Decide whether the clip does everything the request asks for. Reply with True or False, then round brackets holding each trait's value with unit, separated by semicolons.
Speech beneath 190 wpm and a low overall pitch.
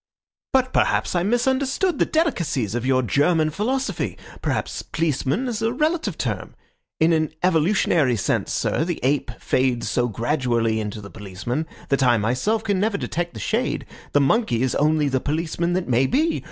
False (165 wpm; 155 Hz)